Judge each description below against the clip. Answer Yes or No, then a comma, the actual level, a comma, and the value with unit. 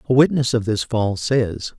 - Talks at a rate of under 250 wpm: Yes, average, 200 wpm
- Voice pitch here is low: Yes, low, 115 Hz